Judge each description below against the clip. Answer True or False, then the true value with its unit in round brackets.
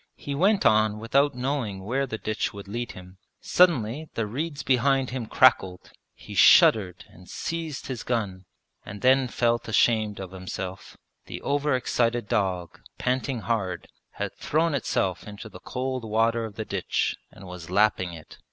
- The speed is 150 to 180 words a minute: True (160 wpm)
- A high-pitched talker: False (115 Hz)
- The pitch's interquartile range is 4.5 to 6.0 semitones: True (5.0 semitones)